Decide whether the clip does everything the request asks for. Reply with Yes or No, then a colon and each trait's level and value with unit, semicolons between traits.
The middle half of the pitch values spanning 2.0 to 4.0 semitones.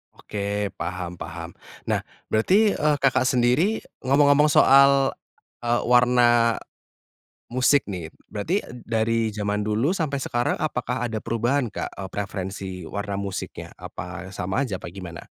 No: average, 5.3 semitones